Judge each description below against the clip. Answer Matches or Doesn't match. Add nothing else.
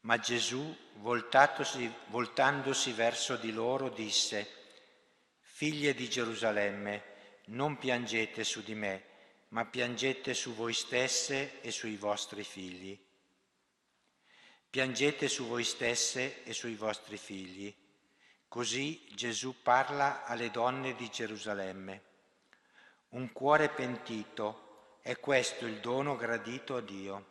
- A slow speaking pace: Matches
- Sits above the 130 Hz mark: Doesn't match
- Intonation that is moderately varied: Matches